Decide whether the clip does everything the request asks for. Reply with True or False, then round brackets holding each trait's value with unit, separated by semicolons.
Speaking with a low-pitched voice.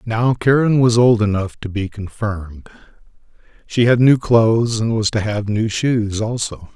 True (110 Hz)